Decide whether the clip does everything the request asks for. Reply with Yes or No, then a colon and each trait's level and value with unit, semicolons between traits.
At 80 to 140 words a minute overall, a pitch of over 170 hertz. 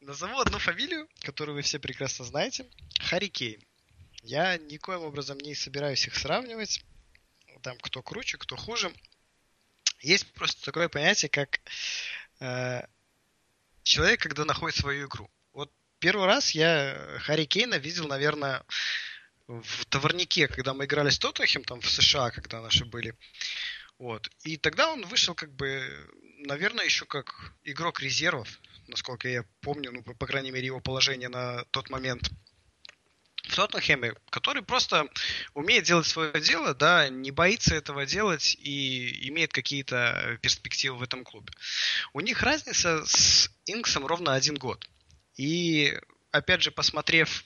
No: average, 135 wpm; medium, 140 Hz